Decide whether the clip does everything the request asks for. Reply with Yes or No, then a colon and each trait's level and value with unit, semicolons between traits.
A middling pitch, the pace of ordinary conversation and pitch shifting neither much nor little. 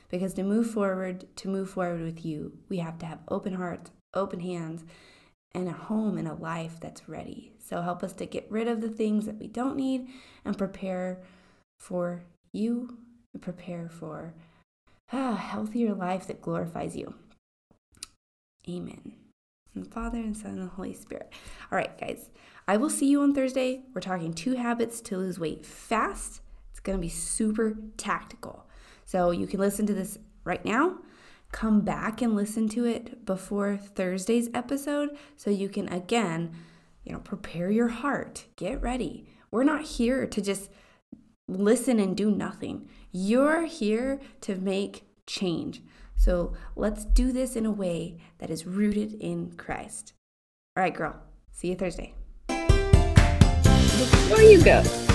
No: high, 200 Hz; average, 160 wpm; average, 4.6 semitones